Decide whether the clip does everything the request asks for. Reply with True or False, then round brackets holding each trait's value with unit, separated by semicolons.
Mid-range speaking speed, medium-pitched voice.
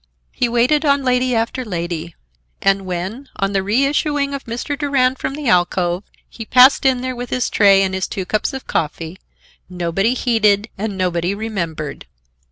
False (170 wpm; 220 Hz)